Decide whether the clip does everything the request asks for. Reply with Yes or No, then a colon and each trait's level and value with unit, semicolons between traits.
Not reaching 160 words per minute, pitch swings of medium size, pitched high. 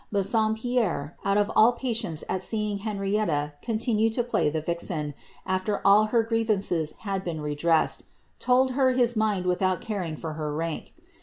Yes: average, 140 wpm; average, 4.9 semitones; high, 195 Hz